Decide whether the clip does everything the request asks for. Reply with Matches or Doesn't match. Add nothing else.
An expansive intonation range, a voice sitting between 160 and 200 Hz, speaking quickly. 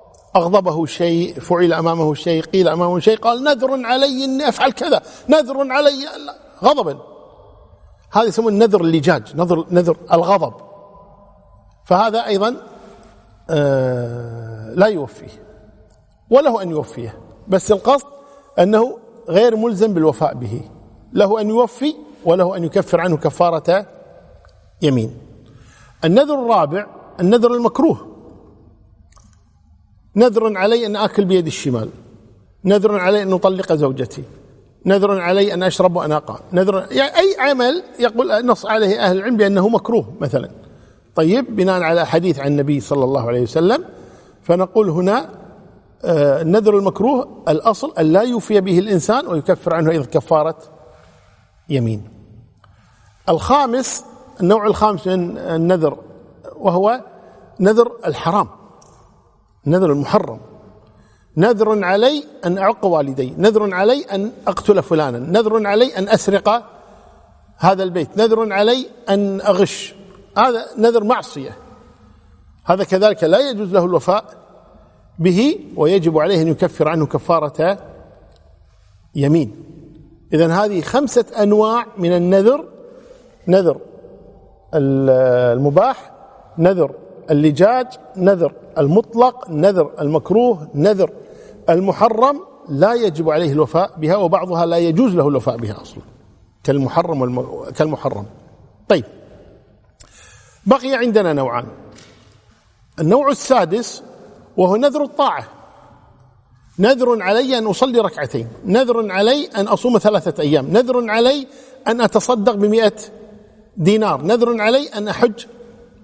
Doesn't match